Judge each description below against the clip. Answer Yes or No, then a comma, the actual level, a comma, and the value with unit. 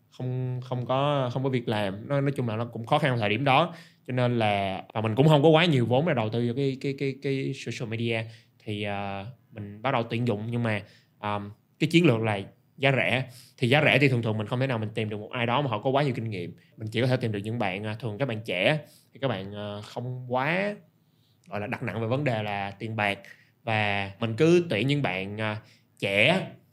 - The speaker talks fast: Yes, fast, 255 wpm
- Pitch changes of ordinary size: Yes, average, 3.9 semitones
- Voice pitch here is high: No, low, 120 Hz